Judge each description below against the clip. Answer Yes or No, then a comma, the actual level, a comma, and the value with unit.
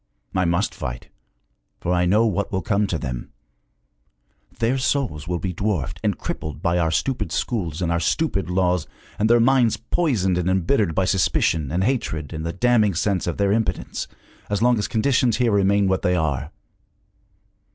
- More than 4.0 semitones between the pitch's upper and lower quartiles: Yes, average, 4.8 semitones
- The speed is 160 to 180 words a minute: Yes, average, 175 wpm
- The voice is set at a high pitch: No, very low, 95 Hz